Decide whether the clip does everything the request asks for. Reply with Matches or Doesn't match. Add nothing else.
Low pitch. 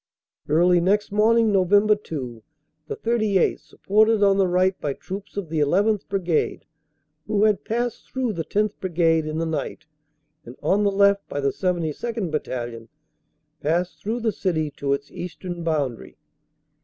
Doesn't match